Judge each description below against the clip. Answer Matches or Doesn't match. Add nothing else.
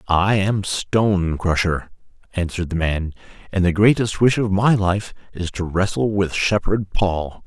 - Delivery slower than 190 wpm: Matches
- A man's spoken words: Matches